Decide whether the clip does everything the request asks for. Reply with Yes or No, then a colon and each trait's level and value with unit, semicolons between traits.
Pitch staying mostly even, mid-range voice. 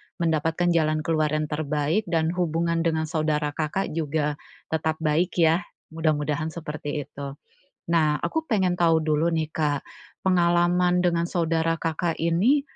Yes: narrow, 2.0 semitones; medium, 160 Hz